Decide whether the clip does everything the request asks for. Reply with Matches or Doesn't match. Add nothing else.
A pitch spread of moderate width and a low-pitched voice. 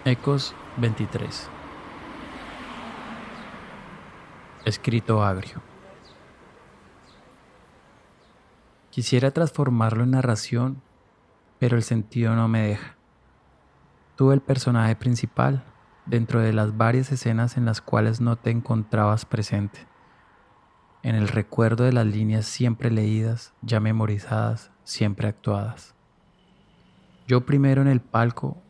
Doesn't match